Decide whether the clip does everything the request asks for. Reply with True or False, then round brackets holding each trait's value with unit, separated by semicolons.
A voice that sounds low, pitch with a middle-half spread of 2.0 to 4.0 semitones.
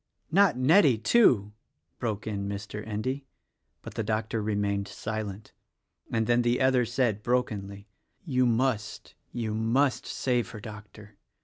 True (110 Hz; 3.3 semitones)